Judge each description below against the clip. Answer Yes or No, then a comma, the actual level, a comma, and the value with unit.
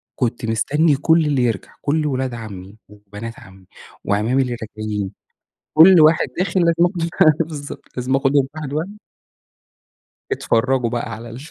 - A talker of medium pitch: No, low, 130 Hz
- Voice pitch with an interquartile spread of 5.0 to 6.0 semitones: Yes, wide, 5.6 semitones